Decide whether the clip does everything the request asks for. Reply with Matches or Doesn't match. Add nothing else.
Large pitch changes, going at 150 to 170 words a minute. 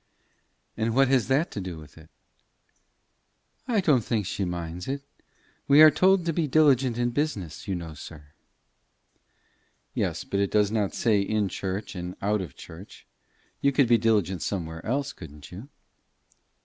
Matches